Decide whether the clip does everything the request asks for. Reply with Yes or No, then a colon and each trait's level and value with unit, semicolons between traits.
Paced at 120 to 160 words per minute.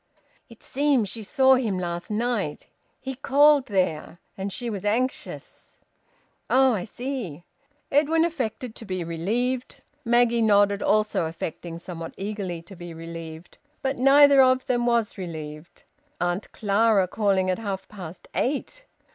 Yes: average, 140 wpm